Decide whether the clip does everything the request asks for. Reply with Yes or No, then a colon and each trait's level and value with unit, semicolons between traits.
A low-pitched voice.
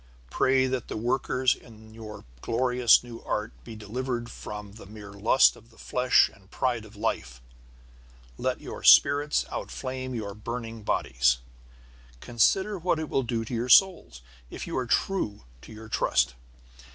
Yes: low, 115 Hz